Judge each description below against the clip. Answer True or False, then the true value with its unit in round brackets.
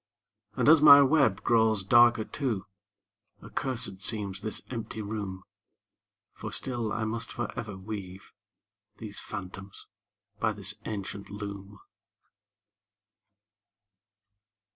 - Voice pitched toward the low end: True (110 Hz)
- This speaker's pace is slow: True (100 wpm)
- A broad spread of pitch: False (3.1 semitones)